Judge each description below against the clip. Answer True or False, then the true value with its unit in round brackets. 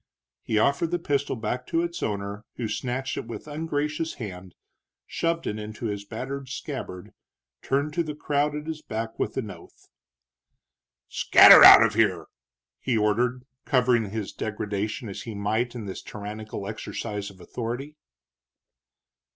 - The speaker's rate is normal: True (150 wpm)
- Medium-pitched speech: False (115 Hz)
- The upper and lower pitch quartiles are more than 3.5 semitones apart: True (5.3 semitones)